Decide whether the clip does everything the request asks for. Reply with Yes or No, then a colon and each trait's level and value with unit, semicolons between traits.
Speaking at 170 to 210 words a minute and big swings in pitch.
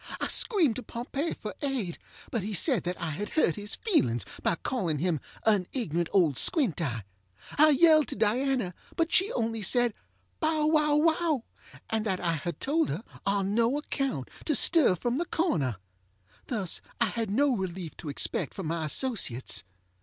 Yes: average, 175 wpm; wide, 8.9 semitones